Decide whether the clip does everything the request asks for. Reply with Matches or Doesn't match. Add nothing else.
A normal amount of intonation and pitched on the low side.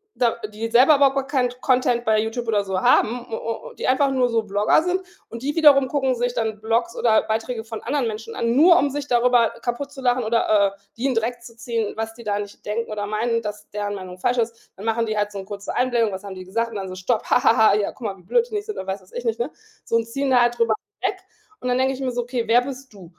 Doesn't match